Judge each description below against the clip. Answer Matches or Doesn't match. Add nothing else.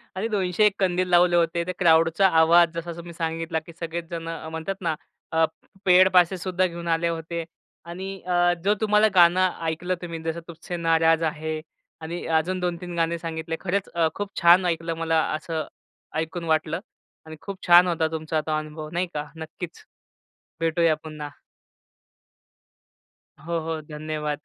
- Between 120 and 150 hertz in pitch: Doesn't match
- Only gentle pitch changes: Matches